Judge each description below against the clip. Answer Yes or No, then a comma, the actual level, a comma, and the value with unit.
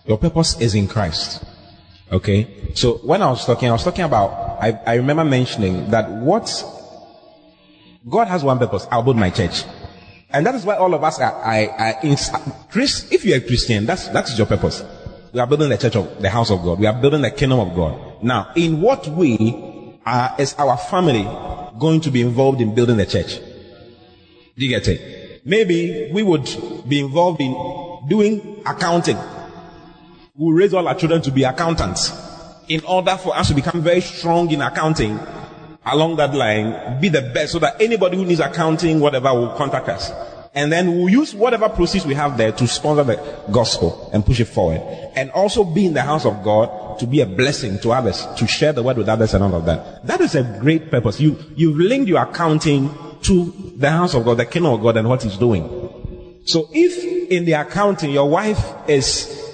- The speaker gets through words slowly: No, average, 200 wpm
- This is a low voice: No, medium, 145 Hz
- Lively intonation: Yes, wide, 6.6 semitones